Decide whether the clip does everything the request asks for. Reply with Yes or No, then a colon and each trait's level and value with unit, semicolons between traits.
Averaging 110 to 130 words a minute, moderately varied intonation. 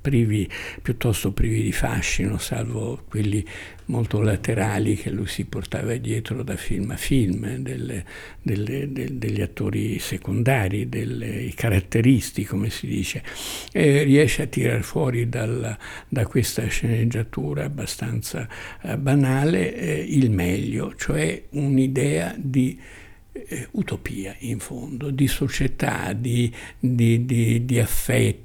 Yes: average, 120 wpm; average, 3.9 semitones